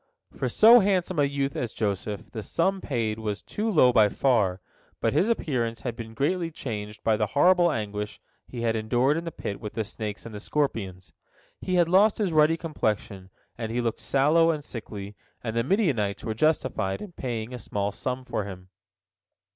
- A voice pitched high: No, low, 120 Hz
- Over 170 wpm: Yes, average, 190 wpm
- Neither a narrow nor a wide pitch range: No, wide, 6.9 semitones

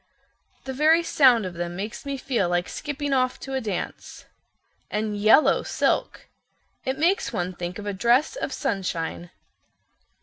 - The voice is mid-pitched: No, high, 230 Hz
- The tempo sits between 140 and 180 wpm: Yes, average, 155 wpm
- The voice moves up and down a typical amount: No, wide, 6.8 semitones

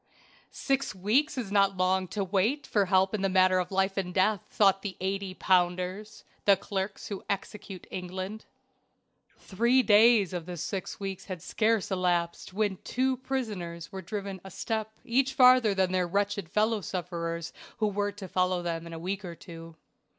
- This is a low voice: No, high, 195 Hz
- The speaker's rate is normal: Yes, average, 170 wpm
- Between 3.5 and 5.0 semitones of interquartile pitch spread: No, narrow, 2.6 semitones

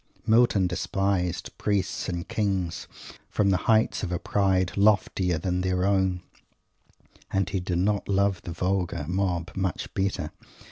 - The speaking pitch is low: Yes, very low, 95 Hz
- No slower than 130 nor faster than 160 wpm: Yes, average, 140 wpm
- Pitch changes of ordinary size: No, narrow, 1.8 semitones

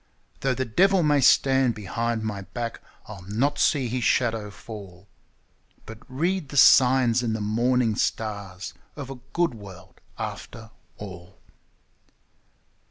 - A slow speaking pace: Yes, slow, 130 wpm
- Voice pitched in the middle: No, low, 115 Hz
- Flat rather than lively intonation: No, average, 4.2 semitones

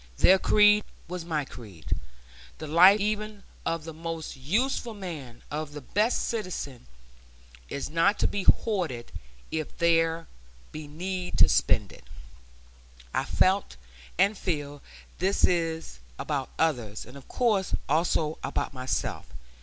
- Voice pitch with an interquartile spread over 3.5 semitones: Yes, average, 4.8 semitones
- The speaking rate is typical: No, slow, 130 wpm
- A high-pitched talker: No, medium, 165 Hz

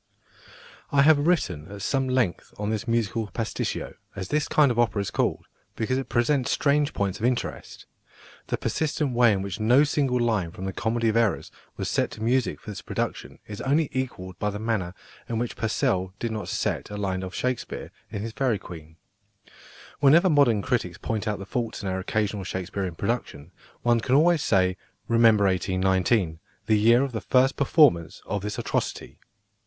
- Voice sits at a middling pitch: No, low, 110 Hz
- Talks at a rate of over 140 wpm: Yes, average, 185 wpm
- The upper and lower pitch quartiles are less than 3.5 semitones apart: No, average, 4.7 semitones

